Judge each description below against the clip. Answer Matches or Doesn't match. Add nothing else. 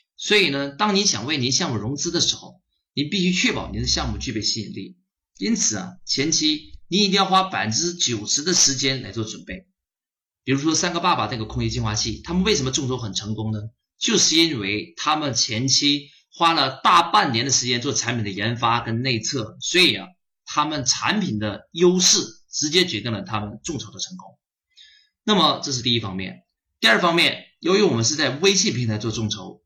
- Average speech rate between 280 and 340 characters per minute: Matches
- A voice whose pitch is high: Doesn't match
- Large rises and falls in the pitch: Matches